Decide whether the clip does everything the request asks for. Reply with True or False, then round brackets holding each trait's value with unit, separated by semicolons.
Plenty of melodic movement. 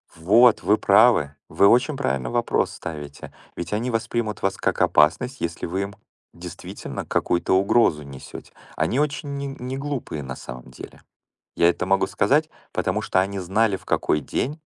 True (7.1 semitones)